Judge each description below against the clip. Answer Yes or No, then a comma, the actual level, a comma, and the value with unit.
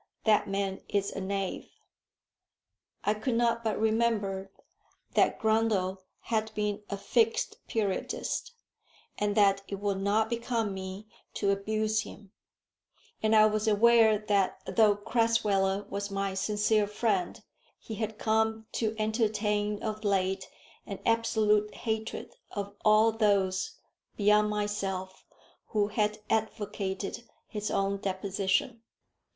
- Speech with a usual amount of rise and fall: No, narrow, 1.8 semitones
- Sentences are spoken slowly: Yes, slow, 120 wpm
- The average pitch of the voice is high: Yes, high, 210 Hz